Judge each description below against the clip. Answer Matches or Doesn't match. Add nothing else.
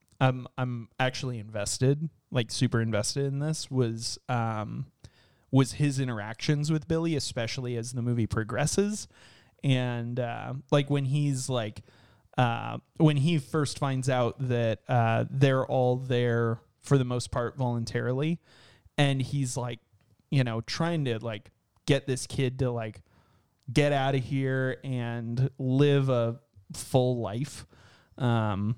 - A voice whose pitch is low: Matches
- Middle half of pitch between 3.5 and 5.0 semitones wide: Doesn't match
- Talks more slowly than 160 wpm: Matches